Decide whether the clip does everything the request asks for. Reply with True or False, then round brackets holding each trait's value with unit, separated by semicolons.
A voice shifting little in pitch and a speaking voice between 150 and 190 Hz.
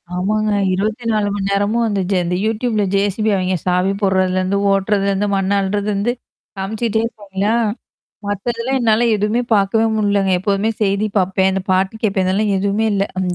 False (2.0 semitones; 200 Hz)